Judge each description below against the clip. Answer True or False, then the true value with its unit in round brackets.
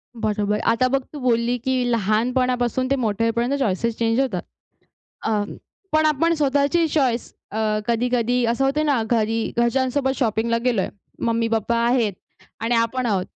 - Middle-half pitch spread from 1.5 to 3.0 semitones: True (2.4 semitones)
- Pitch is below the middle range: False (235 Hz)